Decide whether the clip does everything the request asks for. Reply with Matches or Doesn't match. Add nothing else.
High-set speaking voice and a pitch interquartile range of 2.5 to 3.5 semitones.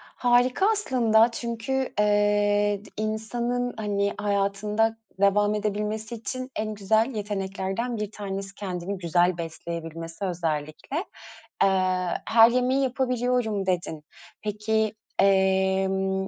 Matches